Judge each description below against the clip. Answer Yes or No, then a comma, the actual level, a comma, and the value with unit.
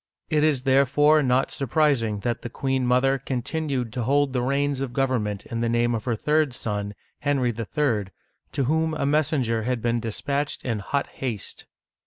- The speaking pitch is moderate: No, low, 130 Hz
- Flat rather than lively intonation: No, average, 3.4 semitones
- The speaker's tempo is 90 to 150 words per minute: No, average, 175 wpm